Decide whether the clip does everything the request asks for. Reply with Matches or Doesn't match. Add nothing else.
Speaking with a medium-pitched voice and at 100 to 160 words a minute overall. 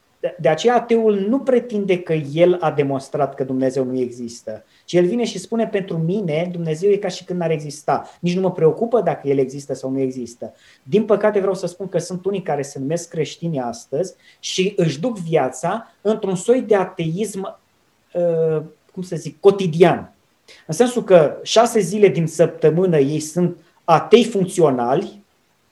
Doesn't match